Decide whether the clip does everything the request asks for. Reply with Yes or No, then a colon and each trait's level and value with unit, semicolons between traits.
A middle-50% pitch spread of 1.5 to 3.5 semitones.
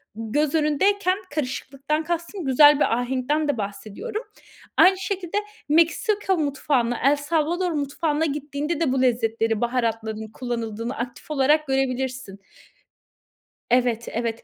No: average, 4.8 semitones